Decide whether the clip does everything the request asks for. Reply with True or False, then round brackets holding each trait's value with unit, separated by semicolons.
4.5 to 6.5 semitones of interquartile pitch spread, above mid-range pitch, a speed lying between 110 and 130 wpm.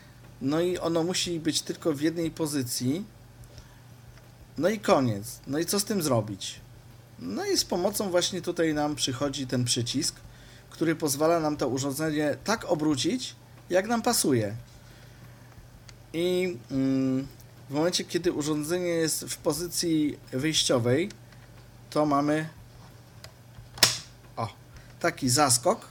False (5.5 semitones; 135 Hz; 120 wpm)